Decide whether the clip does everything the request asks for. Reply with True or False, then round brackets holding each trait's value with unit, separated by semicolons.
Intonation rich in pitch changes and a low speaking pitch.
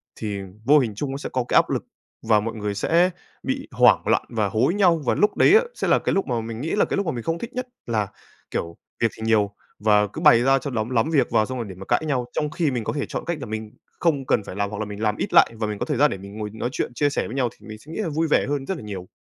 True (5.9 semitones; 120 Hz)